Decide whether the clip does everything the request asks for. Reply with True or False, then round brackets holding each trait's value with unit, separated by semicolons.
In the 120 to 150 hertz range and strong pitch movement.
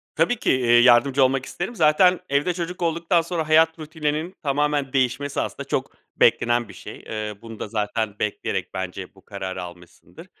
True (140 Hz; 6.5 semitones)